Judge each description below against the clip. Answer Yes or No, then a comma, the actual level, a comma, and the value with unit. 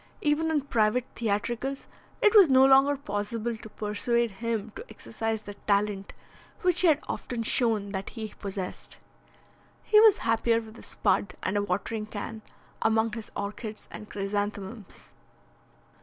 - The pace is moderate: Yes, average, 145 wpm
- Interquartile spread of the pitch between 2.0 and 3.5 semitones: Yes, average, 3.1 semitones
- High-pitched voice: Yes, high, 220 Hz